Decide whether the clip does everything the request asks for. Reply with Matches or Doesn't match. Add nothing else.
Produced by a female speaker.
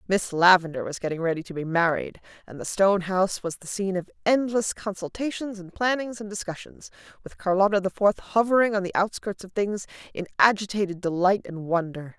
Matches